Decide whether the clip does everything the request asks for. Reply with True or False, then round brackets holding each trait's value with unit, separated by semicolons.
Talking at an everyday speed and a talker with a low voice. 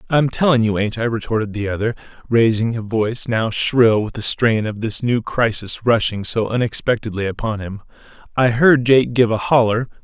True (185 wpm; 115 Hz)